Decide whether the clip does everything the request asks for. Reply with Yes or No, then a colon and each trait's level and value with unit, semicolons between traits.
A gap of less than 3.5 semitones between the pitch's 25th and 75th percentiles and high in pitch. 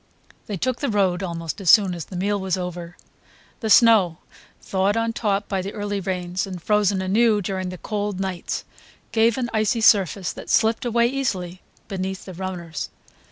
Yes: average, 2.9 semitones; high, 195 Hz